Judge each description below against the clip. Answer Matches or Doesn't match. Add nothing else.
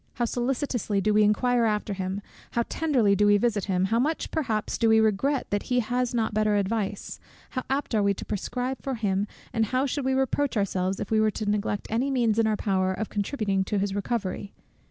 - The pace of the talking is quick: Matches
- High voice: Matches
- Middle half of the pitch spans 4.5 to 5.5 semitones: Doesn't match